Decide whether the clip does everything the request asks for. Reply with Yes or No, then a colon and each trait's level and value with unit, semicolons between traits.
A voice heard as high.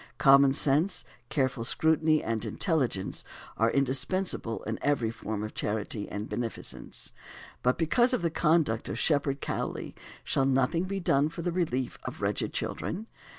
No: low, 135 Hz